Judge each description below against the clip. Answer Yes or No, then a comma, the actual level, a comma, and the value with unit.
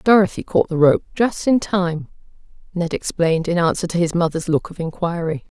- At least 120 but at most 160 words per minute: No, average, 180 wpm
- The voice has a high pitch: No, medium, 175 Hz